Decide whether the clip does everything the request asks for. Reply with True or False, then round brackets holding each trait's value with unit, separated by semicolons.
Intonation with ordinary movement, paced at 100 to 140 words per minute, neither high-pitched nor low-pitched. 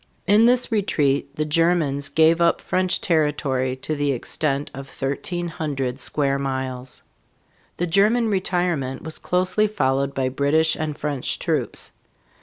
True (4.3 semitones; 135 wpm; 150 Hz)